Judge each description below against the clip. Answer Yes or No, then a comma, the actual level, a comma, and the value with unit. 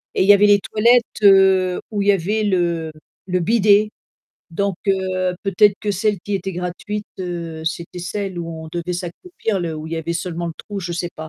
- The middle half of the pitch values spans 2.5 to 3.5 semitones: Yes, average, 2.9 semitones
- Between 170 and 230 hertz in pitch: Yes, medium, 185 Hz